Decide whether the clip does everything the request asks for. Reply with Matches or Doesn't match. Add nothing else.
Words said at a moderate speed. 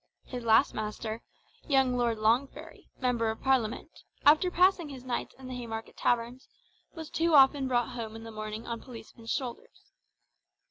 Matches